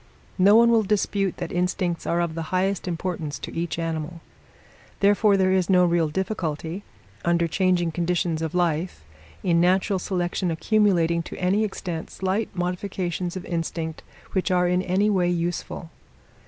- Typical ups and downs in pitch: No, narrow, 2.1 semitones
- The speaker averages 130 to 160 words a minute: Yes, average, 155 wpm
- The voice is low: No, medium, 180 Hz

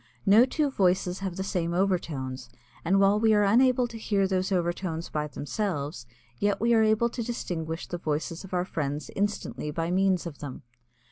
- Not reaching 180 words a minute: No, average, 185 wpm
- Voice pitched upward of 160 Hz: Yes, medium, 185 Hz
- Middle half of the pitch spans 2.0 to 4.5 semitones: Yes, average, 4.2 semitones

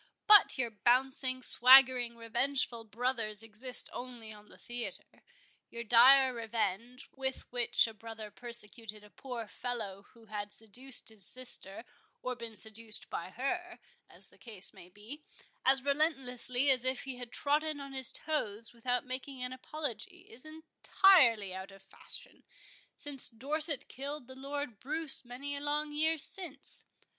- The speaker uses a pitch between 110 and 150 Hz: No, very high, 250 Hz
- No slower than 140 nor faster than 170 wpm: Yes, average, 150 wpm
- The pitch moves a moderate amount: Yes, average, 3.6 semitones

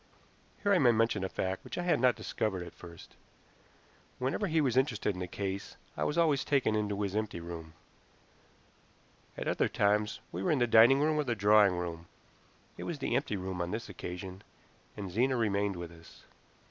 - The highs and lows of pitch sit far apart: Yes, wide, 5.8 semitones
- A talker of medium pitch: No, low, 105 Hz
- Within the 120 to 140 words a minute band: No, average, 195 wpm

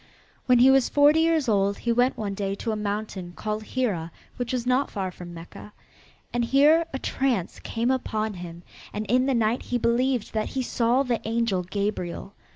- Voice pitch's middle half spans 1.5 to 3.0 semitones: No, average, 4.2 semitones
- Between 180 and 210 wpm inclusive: Yes, average, 190 wpm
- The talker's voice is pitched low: No, high, 230 Hz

